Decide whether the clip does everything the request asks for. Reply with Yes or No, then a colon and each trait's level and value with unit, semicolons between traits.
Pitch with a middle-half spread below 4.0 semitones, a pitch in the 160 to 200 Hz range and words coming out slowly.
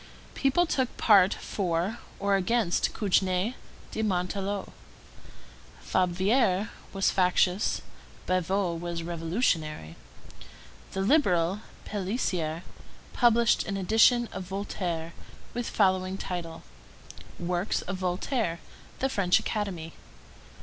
Yes: average, 3.3 semitones; high, 190 Hz; slow, 100 wpm